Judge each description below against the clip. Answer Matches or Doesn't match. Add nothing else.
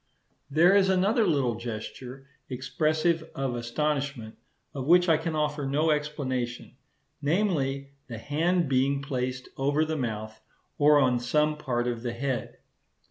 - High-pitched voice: Doesn't match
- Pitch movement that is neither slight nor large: Matches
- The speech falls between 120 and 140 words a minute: Matches